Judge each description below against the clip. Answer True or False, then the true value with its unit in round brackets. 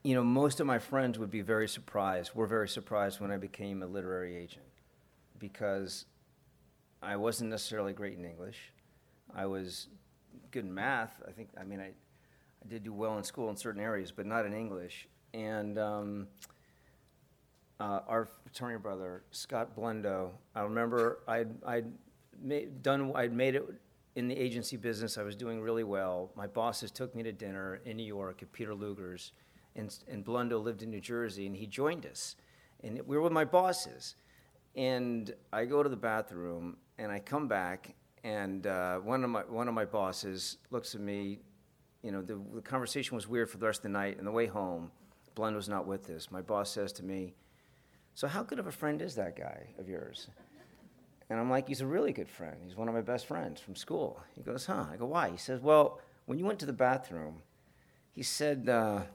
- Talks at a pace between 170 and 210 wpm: True (200 wpm)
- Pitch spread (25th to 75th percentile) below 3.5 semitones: False (3.9 semitones)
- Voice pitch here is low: True (110 Hz)